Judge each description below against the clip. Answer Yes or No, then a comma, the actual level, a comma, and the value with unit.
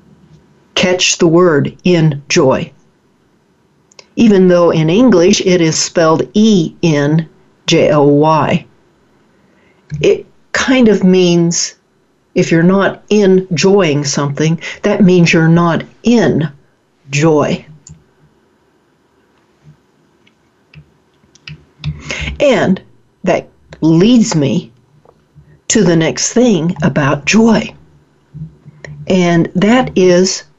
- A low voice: No, medium, 175 Hz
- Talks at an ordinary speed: No, slow, 90 wpm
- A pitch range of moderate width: Yes, average, 3.5 semitones